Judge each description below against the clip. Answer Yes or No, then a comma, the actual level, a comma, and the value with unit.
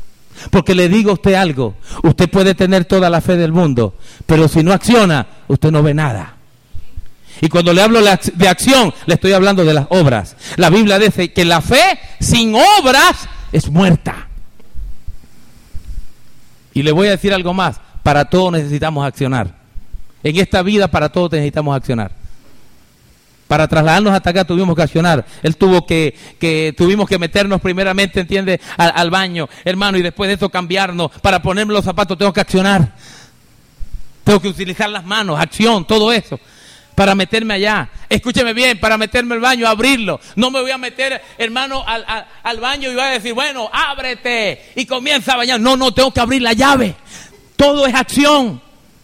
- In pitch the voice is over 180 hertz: Yes, high, 190 Hz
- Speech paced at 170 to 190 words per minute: Yes, average, 175 wpm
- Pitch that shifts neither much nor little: No, wide, 5.7 semitones